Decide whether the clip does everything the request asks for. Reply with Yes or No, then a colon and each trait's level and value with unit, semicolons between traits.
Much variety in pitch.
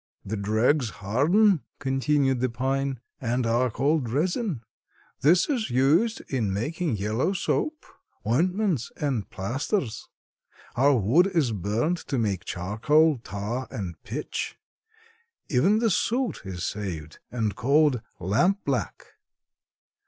Yes: wide, 6.7 semitones